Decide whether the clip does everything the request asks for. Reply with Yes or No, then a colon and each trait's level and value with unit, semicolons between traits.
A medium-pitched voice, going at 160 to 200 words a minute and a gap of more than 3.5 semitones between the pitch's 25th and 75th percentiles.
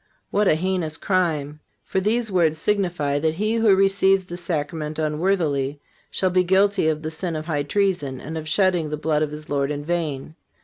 Yes: medium, 160 Hz; average, 190 wpm; average, 3.9 semitones